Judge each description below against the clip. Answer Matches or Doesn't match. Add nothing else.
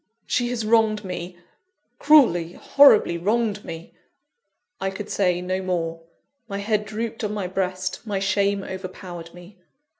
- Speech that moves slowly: Doesn't match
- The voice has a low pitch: Doesn't match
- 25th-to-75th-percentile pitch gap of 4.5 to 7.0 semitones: Doesn't match